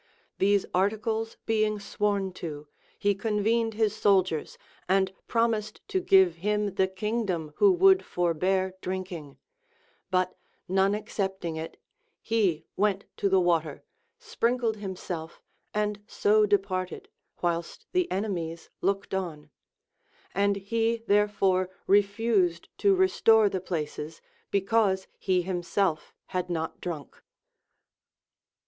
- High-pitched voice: Yes, high, 195 Hz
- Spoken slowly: Yes, slow, 110 wpm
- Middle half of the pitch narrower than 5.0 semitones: Yes, average, 2.9 semitones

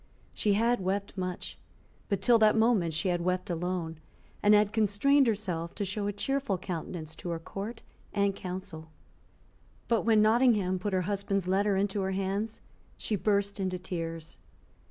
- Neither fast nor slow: Yes, average, 160 wpm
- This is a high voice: Yes, high, 195 Hz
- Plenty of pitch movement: No, average, 2.7 semitones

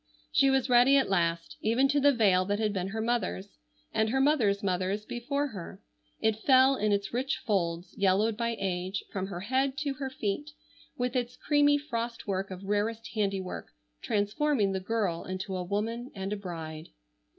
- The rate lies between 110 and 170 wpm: No, average, 180 wpm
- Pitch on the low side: No, high, 215 Hz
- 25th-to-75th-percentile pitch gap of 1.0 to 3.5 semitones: No, average, 4.8 semitones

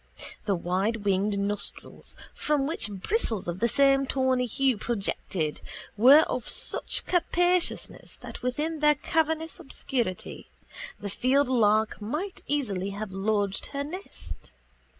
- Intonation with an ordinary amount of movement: No, wide, 6.5 semitones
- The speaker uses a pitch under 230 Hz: No, high, 245 Hz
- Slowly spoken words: Yes, slow, 115 wpm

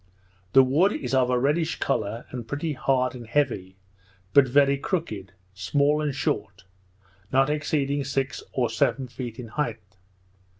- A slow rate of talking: No, average, 145 wpm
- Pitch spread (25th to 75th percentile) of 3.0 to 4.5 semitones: Yes, average, 3.6 semitones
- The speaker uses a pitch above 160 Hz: No, low, 135 Hz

